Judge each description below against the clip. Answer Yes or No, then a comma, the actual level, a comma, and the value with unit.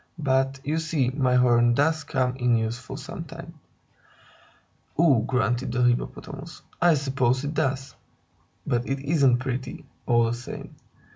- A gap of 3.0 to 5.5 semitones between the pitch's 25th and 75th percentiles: No, narrow, 2.5 semitones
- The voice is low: Yes, low, 130 Hz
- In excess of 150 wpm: No, slow, 135 wpm